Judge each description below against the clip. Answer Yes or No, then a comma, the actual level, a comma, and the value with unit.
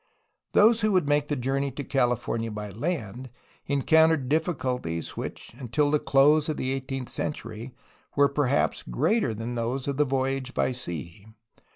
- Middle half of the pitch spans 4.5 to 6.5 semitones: No, average, 3.6 semitones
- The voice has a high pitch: No, low, 135 Hz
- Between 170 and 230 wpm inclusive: No, average, 155 wpm